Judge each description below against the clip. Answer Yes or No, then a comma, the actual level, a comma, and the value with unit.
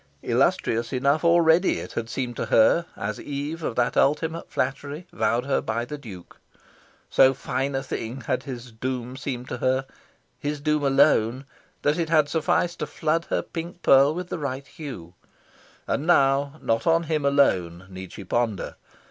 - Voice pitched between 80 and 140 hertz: Yes, low, 135 Hz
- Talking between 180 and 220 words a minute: No, average, 170 wpm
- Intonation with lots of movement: No, average, 4.3 semitones